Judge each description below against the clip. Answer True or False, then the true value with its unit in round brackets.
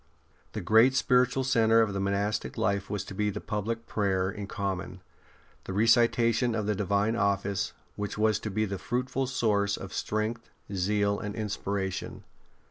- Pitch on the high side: False (105 Hz)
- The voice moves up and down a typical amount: False (2.3 semitones)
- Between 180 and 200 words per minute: False (155 wpm)